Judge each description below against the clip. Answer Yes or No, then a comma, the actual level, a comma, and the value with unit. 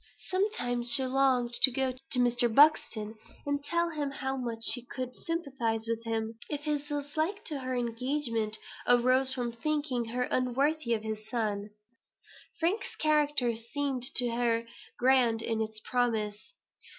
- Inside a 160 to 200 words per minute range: No, average, 145 wpm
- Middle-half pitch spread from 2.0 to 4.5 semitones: Yes, average, 3.7 semitones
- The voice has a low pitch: No, very high, 250 Hz